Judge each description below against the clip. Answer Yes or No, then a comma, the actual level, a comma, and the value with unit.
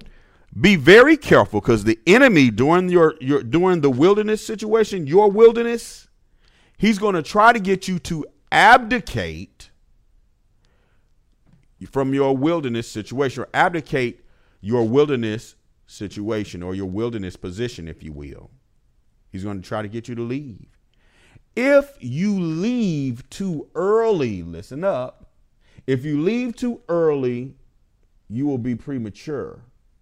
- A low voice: Yes, low, 130 Hz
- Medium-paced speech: No, slow, 130 wpm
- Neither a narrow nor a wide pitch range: No, wide, 8.8 semitones